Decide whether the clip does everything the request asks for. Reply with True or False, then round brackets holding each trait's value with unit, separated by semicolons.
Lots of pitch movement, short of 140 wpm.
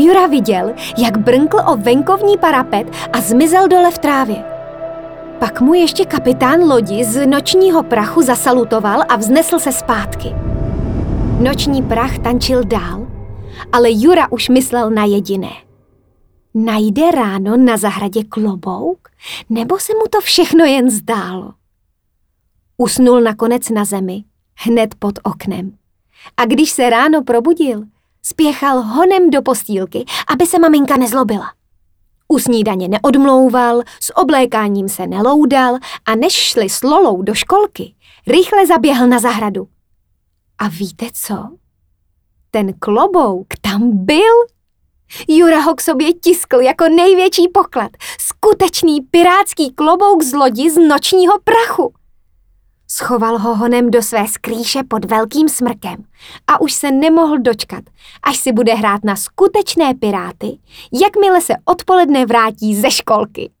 True (7.2 semitones; 125 wpm)